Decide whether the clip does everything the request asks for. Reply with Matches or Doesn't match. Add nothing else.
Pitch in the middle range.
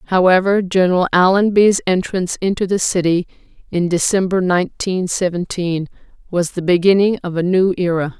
Matches